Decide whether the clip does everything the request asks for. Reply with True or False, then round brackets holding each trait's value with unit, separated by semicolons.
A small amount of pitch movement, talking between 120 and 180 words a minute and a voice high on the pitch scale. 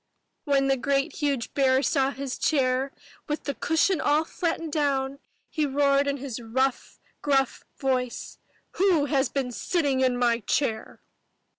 True (1.9 semitones; 150 wpm; 275 Hz)